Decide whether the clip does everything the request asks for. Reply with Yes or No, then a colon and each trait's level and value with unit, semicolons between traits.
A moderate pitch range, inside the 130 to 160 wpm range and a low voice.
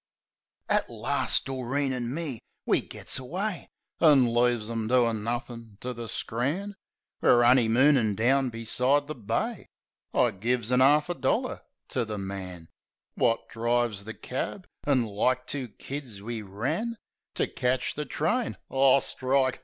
Yes: average, 3.2 semitones; average, 150 wpm; low, 125 Hz